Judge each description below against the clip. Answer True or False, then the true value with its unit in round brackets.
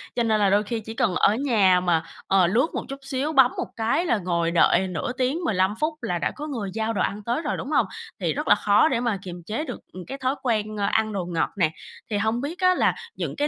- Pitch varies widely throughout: True (5.7 semitones)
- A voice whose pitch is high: True (220 Hz)